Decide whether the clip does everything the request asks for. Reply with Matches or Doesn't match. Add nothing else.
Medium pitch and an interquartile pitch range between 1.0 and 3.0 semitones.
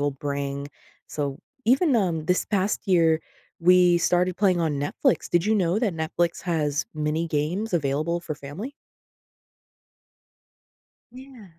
Doesn't match